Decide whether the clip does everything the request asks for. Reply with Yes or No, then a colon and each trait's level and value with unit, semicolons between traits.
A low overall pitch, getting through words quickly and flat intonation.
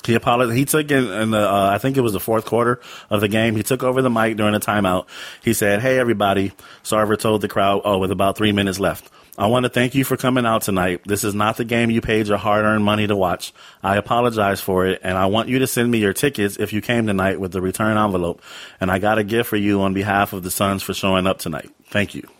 No: low, 105 Hz; fast, 270 wpm; average, 3.0 semitones